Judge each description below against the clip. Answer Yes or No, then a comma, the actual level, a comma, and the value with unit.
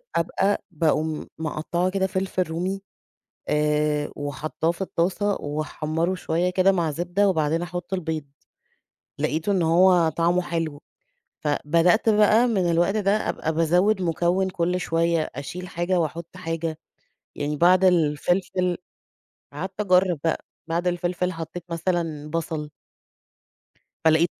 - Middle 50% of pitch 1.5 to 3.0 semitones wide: Yes, narrow, 2.4 semitones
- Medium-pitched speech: Yes, medium, 170 Hz